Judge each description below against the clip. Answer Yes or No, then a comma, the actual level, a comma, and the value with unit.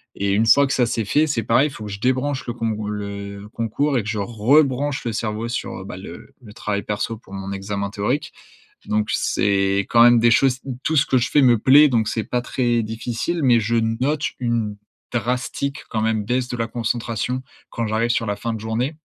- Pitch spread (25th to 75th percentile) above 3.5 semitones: No, average, 3.2 semitones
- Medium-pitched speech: No, low, 115 Hz